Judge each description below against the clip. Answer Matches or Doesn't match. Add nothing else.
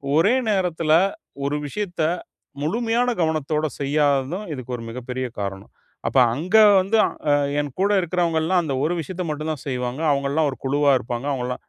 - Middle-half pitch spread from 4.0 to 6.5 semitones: Matches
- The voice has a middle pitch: Matches